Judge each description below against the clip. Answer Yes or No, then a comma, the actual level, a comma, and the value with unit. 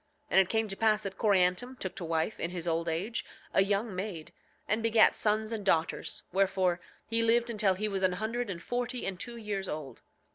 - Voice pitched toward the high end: Yes, high, 200 Hz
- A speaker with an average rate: No, fast, 210 wpm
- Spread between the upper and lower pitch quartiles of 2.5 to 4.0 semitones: Yes, average, 3.6 semitones